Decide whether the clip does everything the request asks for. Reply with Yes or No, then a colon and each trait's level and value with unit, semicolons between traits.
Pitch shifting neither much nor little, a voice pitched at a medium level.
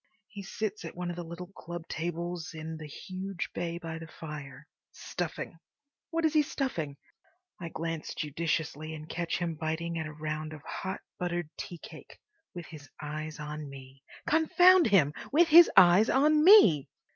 Yes: average, 3.5 semitones; medium, 170 Hz